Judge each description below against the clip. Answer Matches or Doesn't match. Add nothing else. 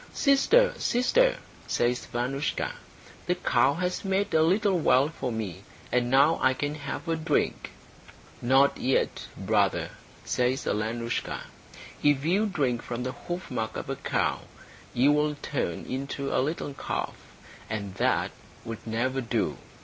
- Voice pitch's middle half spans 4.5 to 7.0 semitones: Matches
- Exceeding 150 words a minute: Doesn't match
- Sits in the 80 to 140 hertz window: Matches